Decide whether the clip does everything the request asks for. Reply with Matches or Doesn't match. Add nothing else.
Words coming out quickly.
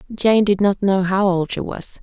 Matches